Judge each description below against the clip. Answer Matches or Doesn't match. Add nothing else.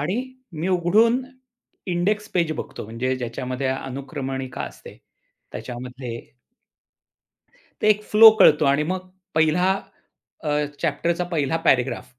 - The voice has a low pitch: Doesn't match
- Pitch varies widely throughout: Matches